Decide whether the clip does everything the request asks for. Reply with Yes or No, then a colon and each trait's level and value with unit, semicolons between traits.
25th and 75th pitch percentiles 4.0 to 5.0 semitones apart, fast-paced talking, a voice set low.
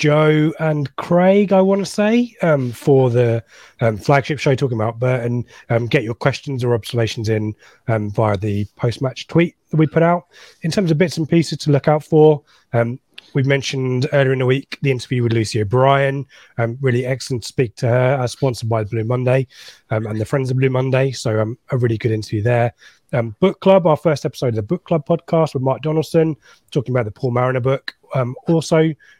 Yes: average, 4.5 semitones; fast, 215 wpm; low, 130 Hz